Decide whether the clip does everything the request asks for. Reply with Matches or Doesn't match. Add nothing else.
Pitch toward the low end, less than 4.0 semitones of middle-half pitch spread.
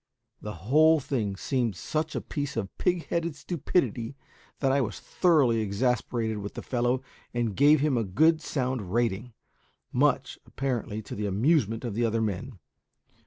Doesn't match